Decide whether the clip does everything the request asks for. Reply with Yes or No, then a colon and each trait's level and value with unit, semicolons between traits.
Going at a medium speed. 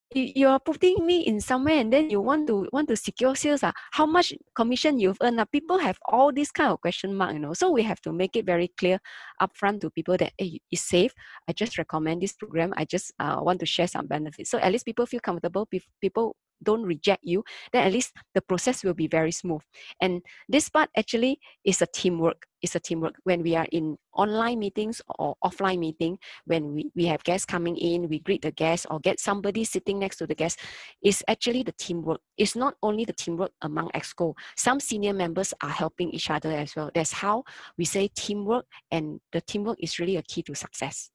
No: fast, 220 wpm